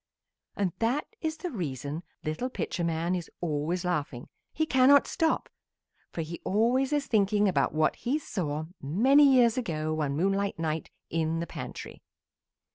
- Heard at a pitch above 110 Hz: Yes, medium, 185 Hz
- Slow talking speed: No, average, 150 wpm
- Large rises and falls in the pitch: Yes, wide, 8.2 semitones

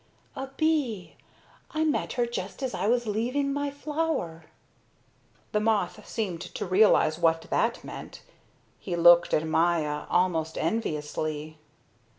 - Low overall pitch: No, high, 190 Hz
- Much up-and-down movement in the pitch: Yes, wide, 7.2 semitones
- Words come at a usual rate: No, slow, 130 wpm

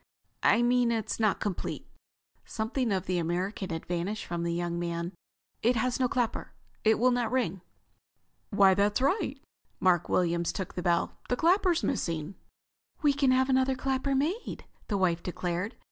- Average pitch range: No, wide, 6.6 semitones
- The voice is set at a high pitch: Yes, high, 215 Hz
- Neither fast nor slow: Yes, average, 165 wpm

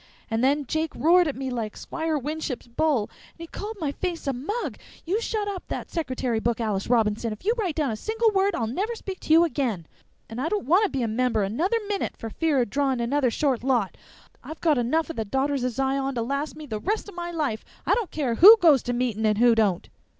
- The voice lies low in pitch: No, very high, 280 Hz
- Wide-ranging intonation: Yes, wide, 6.1 semitones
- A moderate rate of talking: No, fast, 240 wpm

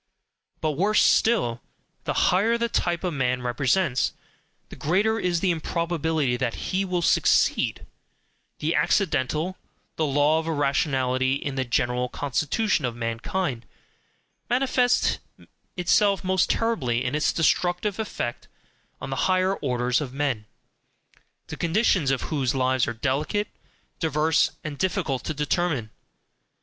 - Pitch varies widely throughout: Yes, wide, 6.1 semitones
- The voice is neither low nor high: Yes, medium, 155 Hz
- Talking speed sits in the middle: No, slow, 130 wpm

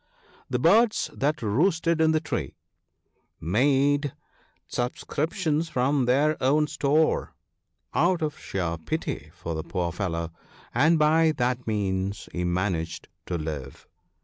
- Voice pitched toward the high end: No, low, 130 Hz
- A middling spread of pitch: No, wide, 8.7 semitones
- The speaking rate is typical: No, slow, 120 wpm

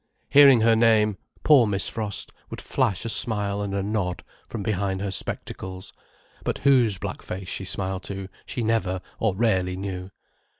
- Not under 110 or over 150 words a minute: No, average, 165 wpm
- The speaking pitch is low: Yes, low, 100 Hz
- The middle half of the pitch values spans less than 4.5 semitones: Yes, average, 3.0 semitones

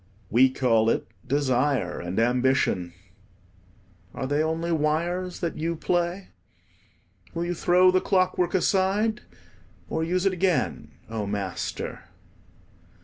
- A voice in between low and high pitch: Yes, medium, 160 Hz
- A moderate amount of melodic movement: No, wide, 6.1 semitones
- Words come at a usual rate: No, slow, 115 wpm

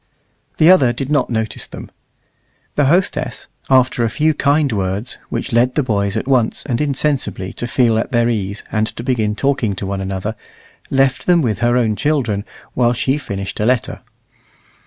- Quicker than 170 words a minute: Yes, average, 180 wpm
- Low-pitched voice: Yes, low, 120 Hz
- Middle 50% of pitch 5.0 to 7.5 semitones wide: No, average, 4.3 semitones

